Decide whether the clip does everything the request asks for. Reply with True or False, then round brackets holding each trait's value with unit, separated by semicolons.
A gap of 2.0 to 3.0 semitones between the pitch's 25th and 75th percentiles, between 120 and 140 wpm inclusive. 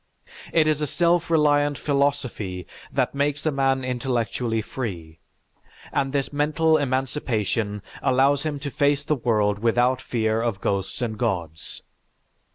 False (4.7 semitones; 135 wpm)